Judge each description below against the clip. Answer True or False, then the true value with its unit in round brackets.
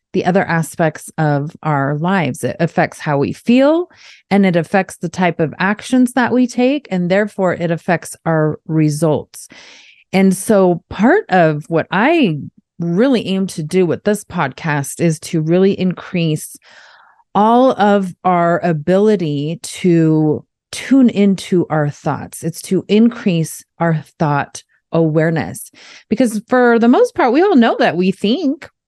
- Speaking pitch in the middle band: True (180 Hz)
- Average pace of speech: True (145 wpm)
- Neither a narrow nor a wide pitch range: True (4.8 semitones)